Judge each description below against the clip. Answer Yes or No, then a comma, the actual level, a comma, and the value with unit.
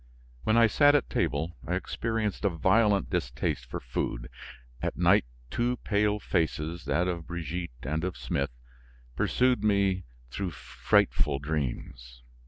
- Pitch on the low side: Yes, very low, 90 Hz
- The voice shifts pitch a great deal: Yes, wide, 5.9 semitones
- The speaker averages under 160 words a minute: Yes, slow, 135 wpm